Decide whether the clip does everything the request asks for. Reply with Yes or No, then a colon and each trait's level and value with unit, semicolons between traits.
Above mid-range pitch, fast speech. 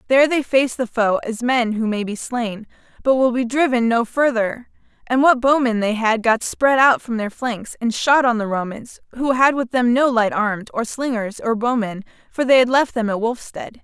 Yes: high, 240 Hz; fast, 225 wpm